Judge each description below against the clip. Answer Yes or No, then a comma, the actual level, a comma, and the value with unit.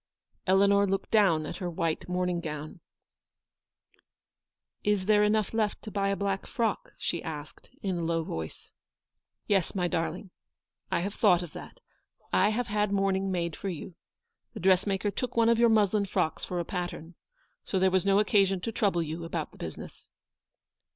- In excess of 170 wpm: Yes, average, 180 wpm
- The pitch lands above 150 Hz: Yes, high, 190 Hz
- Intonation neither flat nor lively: Yes, average, 3.2 semitones